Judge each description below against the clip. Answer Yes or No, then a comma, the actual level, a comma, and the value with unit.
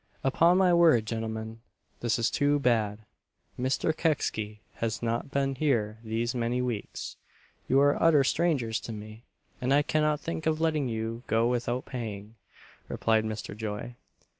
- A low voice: Yes, low, 120 Hz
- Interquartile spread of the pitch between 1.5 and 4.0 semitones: No, average, 4.4 semitones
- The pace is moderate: Yes, average, 150 wpm